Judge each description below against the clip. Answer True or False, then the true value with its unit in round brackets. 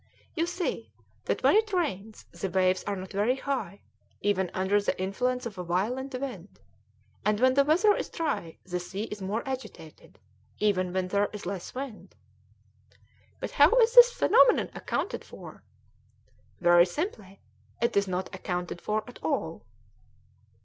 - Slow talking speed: False (155 wpm)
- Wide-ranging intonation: True (6.0 semitones)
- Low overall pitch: False (205 Hz)